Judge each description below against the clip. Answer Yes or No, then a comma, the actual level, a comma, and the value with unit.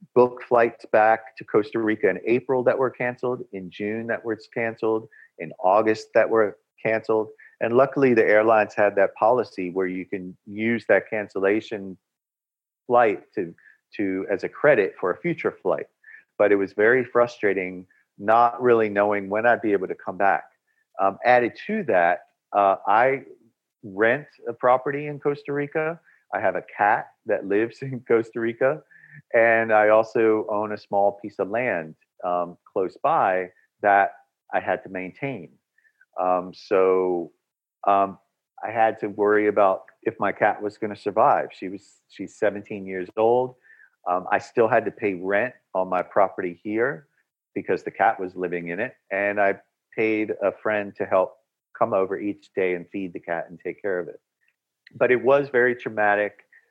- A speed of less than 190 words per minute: Yes, average, 170 wpm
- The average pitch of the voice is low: Yes, low, 110 Hz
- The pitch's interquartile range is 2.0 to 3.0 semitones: No, average, 3.7 semitones